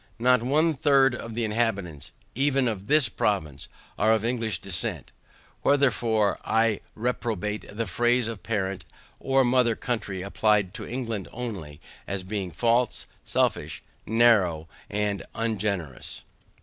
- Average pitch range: Yes, average, 3.6 semitones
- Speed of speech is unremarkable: No, slow, 125 wpm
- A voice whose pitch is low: Yes, low, 110 Hz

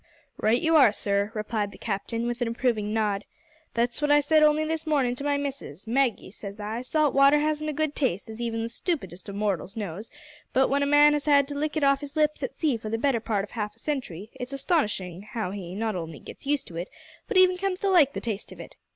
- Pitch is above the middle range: Yes, high, 245 Hz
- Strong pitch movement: Yes, wide, 5.8 semitones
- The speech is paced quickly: Yes, fast, 245 wpm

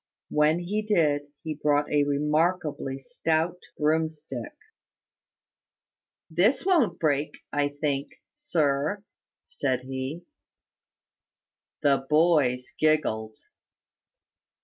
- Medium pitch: Yes, medium, 150 Hz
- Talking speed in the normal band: No, slow, 80 wpm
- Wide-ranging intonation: No, average, 3.1 semitones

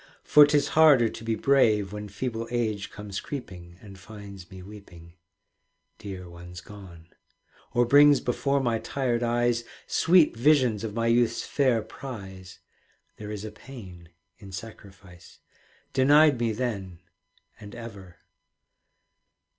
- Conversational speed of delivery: No, slow, 130 wpm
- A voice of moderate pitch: No, low, 110 Hz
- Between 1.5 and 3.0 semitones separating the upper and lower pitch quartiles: No, average, 4.2 semitones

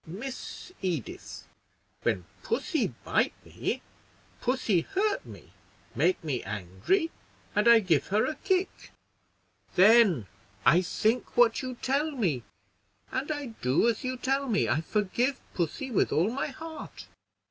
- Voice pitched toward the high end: Yes, high, 230 Hz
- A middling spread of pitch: No, wide, 7.7 semitones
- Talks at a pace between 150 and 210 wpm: No, slow, 135 wpm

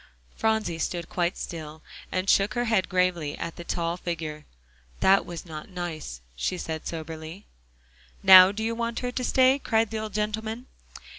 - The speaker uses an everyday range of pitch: Yes, average, 5.0 semitones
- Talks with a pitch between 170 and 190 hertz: Yes, medium, 185 Hz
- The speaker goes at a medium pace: Yes, average, 165 wpm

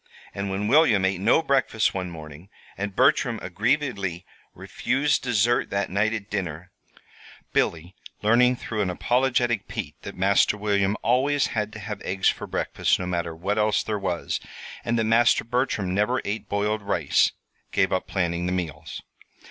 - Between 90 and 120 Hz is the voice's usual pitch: Yes, low, 105 Hz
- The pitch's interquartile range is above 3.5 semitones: Yes, average, 4.2 semitones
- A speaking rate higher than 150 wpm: Yes, average, 160 wpm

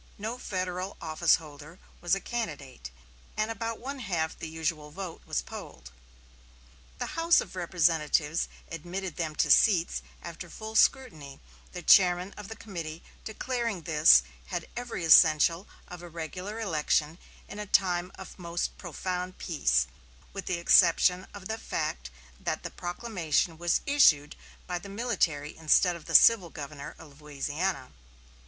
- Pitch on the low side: No, medium, 175 Hz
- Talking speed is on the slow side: No, average, 145 wpm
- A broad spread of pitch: No, average, 4.0 semitones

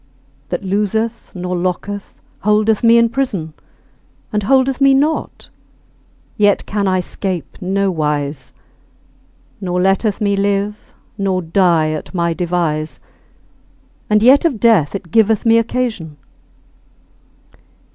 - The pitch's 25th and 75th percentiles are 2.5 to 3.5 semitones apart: No, average, 4.0 semitones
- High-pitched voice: Yes, high, 200 Hz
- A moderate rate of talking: No, slow, 115 wpm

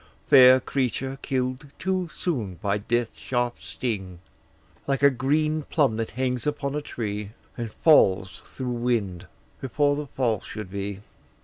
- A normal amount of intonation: Yes, average, 4.6 semitones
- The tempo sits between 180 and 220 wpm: No, average, 140 wpm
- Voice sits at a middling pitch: No, low, 125 Hz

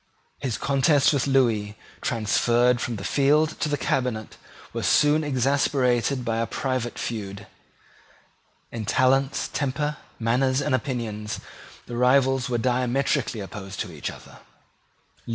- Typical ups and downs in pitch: Yes, average, 3.1 semitones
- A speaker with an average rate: No, slow, 125 wpm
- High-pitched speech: No, low, 125 Hz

